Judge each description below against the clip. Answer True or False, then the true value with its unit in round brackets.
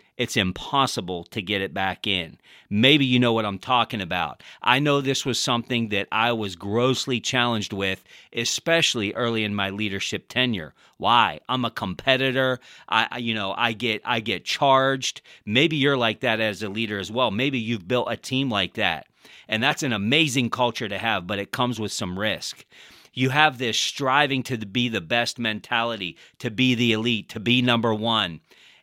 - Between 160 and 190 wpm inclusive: True (185 wpm)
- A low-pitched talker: True (115 Hz)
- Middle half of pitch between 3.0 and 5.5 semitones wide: True (3.3 semitones)